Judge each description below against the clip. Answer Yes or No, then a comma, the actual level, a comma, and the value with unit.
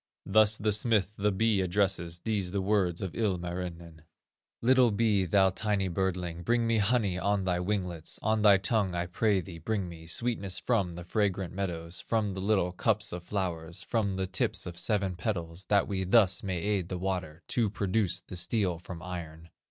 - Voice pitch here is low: Yes, very low, 95 Hz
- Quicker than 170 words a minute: Yes, average, 185 wpm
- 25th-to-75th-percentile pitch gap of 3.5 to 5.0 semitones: No, average, 3.0 semitones